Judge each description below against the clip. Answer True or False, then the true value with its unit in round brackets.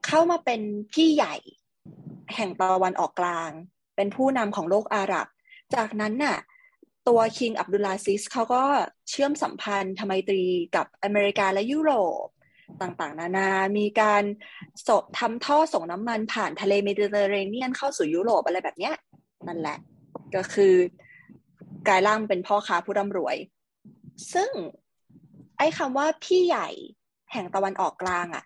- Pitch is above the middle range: True (205 Hz)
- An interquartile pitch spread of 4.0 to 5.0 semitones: False (5.5 semitones)